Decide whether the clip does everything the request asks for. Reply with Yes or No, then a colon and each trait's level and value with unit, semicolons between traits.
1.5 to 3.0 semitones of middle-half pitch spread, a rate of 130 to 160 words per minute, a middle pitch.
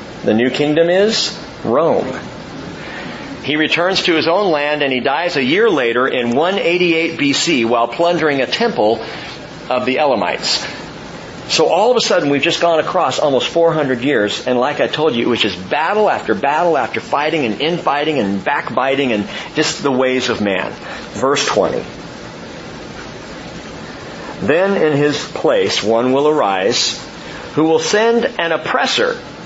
No: average, 4.8 semitones; average, 155 wpm; medium, 150 Hz